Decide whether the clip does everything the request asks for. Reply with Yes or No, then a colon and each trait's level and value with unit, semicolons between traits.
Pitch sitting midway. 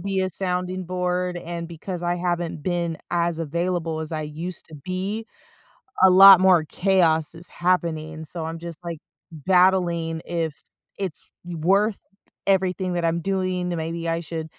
Yes: medium, 175 Hz